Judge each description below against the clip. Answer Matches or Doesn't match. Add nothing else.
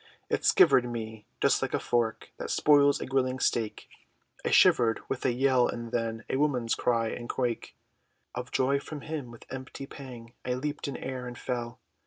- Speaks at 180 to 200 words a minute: Matches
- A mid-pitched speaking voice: Doesn't match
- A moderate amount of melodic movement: Doesn't match